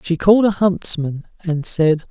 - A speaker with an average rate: Yes, average, 170 wpm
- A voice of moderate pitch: Yes, medium, 175 Hz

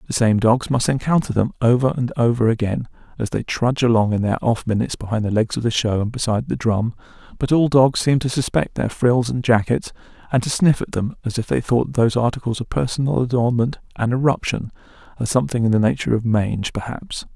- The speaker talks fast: Yes, fast, 210 wpm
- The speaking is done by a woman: No, male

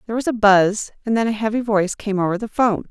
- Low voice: No, high, 215 Hz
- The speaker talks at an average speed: No, fast, 270 wpm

